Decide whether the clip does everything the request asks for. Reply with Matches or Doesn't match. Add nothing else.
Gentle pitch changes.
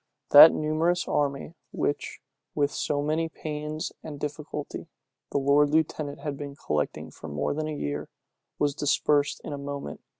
Matches